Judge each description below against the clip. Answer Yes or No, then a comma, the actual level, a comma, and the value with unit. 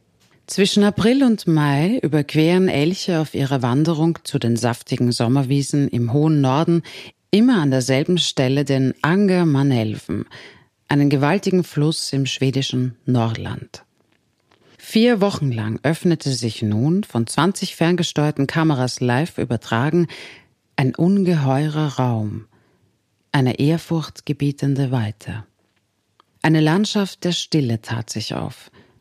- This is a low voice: No, medium, 145 Hz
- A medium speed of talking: No, slow, 110 wpm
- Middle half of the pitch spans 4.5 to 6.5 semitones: Yes, average, 5.3 semitones